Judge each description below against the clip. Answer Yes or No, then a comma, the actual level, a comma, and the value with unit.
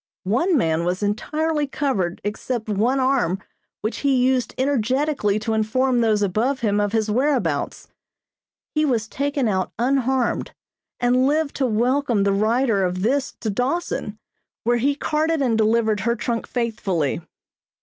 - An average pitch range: Yes, average, 4.4 semitones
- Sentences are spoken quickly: No, average, 145 wpm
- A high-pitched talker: Yes, high, 235 Hz